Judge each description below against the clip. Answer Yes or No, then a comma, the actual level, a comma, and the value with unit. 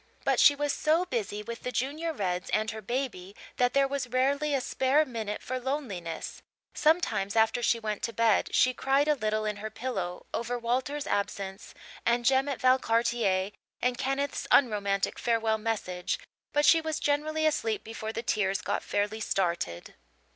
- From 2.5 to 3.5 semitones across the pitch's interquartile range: No, average, 4.6 semitones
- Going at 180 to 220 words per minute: No, average, 170 wpm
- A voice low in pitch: No, high, 235 Hz